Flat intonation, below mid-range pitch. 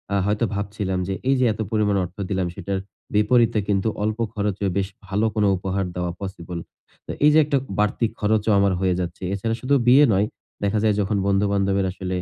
Yes: narrow, 2.1 semitones; low, 100 Hz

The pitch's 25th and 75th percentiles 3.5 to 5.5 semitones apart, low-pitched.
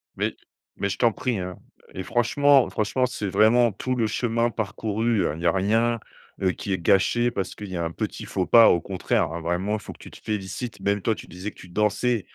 Yes: average, 4.0 semitones; low, 105 Hz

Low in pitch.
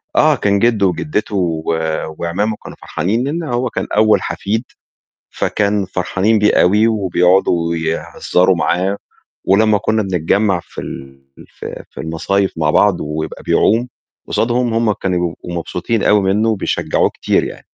Yes: low, 100 Hz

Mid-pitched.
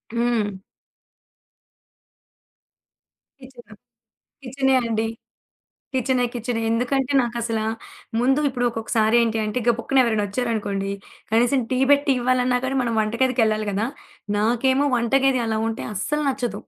No: high, 240 Hz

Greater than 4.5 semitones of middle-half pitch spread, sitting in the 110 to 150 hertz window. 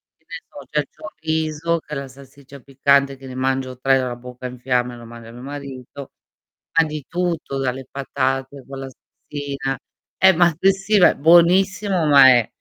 No: average, 3.3 semitones; medium, 140 Hz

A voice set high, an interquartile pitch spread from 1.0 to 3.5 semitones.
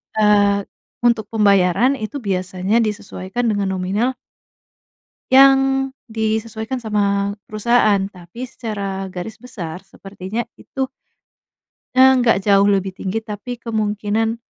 Yes: high, 210 Hz; average, 2.9 semitones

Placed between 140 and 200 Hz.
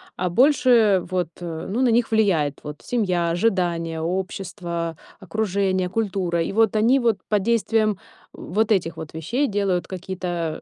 Yes: high, 190 Hz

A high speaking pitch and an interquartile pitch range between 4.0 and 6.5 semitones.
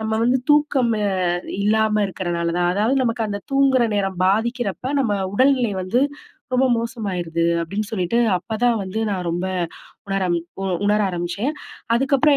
Yes: high, 215 Hz; average, 4.6 semitones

